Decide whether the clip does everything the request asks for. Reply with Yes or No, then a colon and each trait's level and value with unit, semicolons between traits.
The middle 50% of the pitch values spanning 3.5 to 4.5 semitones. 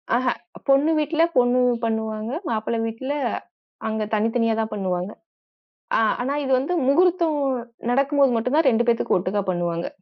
Yes: average, 4.2 semitones